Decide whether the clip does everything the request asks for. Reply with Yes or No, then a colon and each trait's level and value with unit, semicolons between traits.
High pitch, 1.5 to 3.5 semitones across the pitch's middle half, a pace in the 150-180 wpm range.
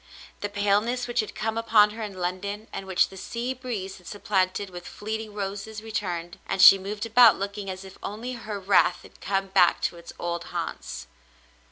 No: high, 205 Hz; narrow, 2.5 semitones; average, 190 wpm